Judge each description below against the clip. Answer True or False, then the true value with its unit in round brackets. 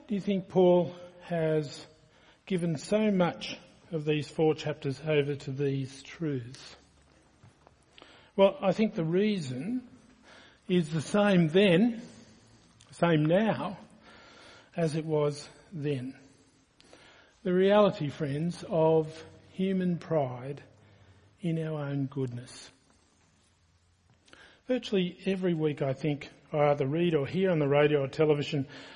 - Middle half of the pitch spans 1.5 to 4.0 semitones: False (4.7 semitones)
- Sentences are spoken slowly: True (115 wpm)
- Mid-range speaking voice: True (155 Hz)